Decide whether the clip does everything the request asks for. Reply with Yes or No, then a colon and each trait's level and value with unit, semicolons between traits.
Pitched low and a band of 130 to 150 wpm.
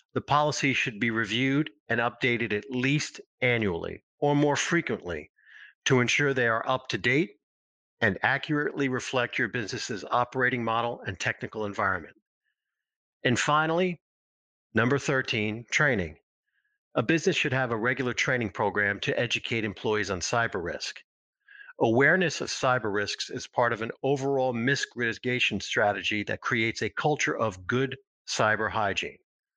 Yes: low, 125 Hz; average, 140 wpm